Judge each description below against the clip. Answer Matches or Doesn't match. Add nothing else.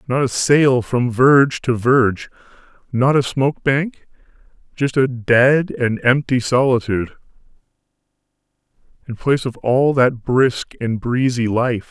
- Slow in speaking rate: Matches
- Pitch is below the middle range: Matches